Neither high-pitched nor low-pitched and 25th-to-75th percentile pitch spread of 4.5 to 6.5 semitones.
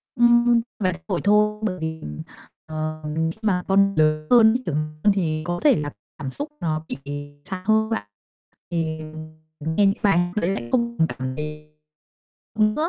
Yes: medium, 175 Hz; average, 5.2 semitones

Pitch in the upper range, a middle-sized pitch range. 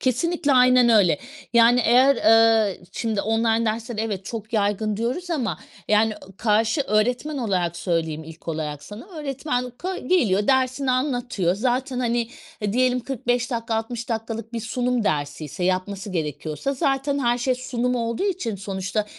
Yes: high, 230 Hz; average, 3.7 semitones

